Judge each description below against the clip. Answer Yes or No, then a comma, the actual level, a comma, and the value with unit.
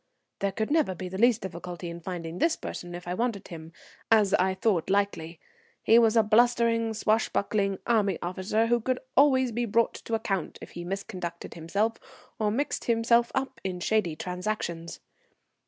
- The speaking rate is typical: Yes, average, 170 wpm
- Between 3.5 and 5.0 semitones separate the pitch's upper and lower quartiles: Yes, average, 4.3 semitones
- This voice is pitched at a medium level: No, high, 205 Hz